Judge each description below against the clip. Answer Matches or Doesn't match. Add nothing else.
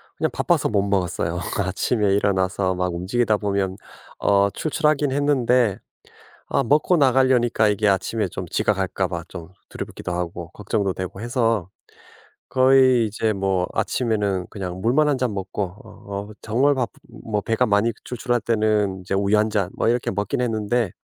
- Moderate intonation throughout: Matches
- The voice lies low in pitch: Matches